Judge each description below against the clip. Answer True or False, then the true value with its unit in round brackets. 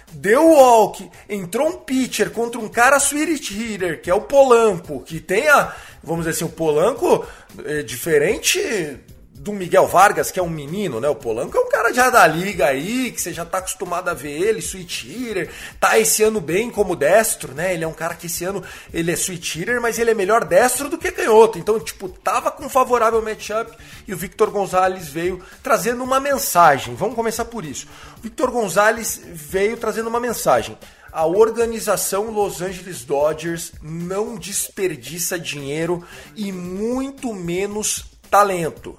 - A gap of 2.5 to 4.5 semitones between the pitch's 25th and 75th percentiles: False (5.1 semitones)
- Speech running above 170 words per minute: True (180 wpm)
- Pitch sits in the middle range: False (205 Hz)